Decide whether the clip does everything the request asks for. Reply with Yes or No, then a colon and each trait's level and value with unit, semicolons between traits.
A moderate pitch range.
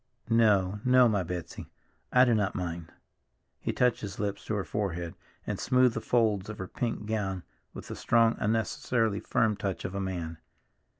Yes: average, 3.3 semitones